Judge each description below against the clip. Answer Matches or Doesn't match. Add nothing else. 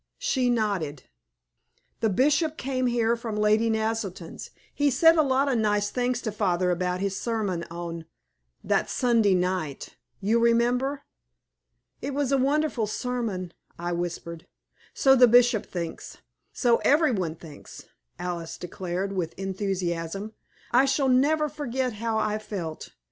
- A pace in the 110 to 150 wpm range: Matches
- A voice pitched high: Matches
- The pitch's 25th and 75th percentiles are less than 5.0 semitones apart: Doesn't match